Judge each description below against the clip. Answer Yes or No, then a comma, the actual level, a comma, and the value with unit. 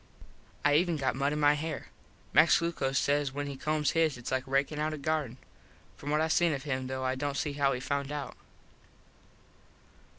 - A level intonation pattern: Yes, narrow, 2.2 semitones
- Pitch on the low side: No, medium, 145 Hz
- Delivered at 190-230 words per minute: Yes, average, 200 wpm